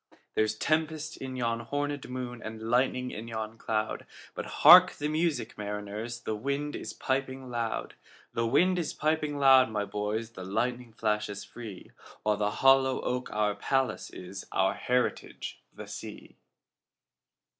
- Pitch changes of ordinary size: Yes, average, 3.9 semitones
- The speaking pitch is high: No, low, 120 Hz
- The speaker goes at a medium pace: No, slow, 125 wpm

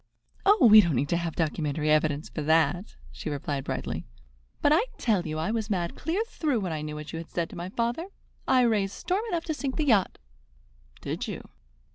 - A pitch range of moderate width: No, wide, 8.1 semitones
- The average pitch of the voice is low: No, medium, 180 Hz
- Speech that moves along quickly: Yes, fast, 210 wpm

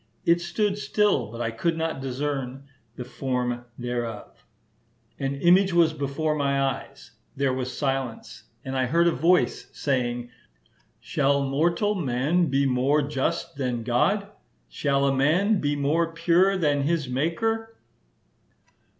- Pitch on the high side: No, medium, 140 Hz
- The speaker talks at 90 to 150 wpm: Yes, slow, 135 wpm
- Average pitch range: Yes, average, 4.4 semitones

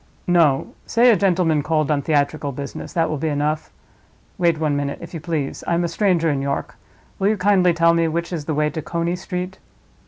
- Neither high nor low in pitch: Yes, medium, 165 Hz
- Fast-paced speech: Yes, fast, 210 wpm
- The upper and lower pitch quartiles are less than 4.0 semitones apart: Yes, average, 3.0 semitones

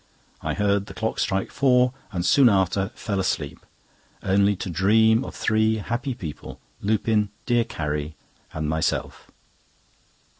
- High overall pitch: No, low, 100 Hz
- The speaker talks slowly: Yes, slow, 125 wpm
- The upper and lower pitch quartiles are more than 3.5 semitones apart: No, average, 3.0 semitones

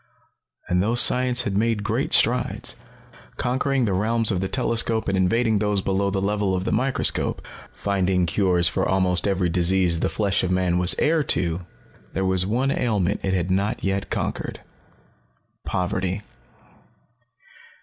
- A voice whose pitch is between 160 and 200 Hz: No, very low, 95 Hz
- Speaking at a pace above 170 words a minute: No, average, 150 wpm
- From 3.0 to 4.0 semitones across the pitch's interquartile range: Yes, average, 3.3 semitones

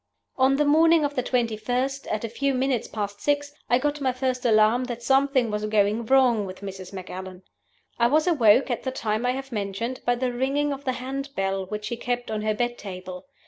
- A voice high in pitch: Yes, high, 245 Hz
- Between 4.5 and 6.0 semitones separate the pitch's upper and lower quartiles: No, average, 4.1 semitones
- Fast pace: Yes, fast, 215 wpm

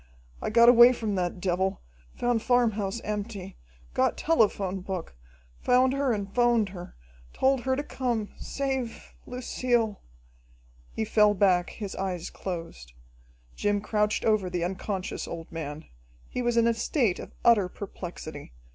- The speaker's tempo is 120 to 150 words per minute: Yes, average, 140 wpm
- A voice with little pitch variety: No, average, 4.3 semitones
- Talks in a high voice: Yes, high, 210 Hz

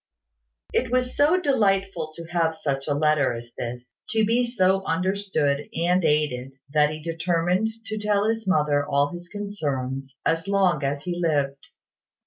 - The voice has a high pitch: No, medium, 165 Hz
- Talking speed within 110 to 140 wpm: No, average, 155 wpm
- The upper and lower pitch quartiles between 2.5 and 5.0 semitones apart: No, wide, 5.6 semitones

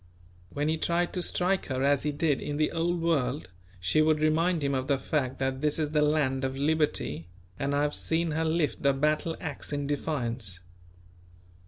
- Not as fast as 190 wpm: No, average, 195 wpm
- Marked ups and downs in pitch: No, average, 2.8 semitones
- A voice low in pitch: No, medium, 150 Hz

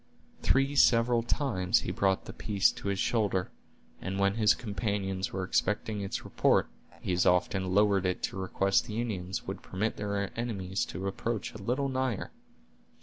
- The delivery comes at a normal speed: Yes, average, 165 wpm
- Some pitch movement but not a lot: Yes, average, 3.2 semitones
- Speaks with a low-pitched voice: Yes, low, 100 Hz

